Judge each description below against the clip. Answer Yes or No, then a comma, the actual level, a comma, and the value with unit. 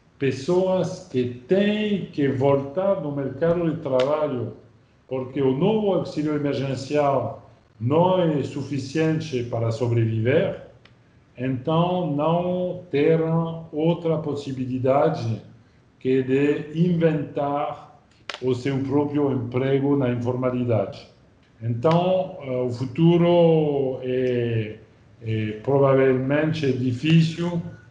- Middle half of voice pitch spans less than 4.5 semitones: Yes, average, 4.1 semitones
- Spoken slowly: Yes, slow, 90 wpm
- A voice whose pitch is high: No, medium, 140 Hz